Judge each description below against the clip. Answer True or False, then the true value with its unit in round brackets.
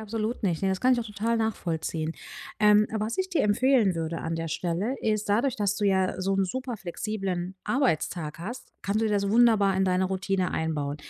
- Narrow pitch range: False (3.4 semitones)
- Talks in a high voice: True (200 Hz)